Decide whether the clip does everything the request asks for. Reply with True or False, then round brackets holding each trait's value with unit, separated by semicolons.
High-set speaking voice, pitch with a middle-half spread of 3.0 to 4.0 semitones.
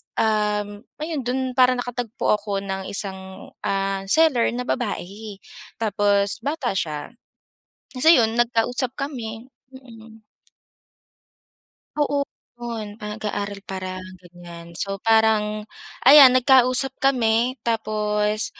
True (220 Hz; 3.7 semitones)